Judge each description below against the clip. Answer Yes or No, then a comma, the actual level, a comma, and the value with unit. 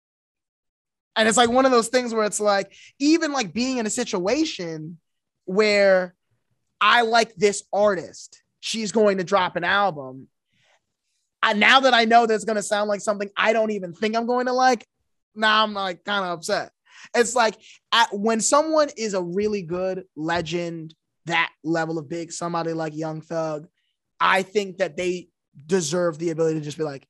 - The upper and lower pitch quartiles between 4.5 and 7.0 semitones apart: Yes, average, 4.9 semitones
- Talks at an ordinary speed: Yes, average, 180 wpm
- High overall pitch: Yes, high, 195 Hz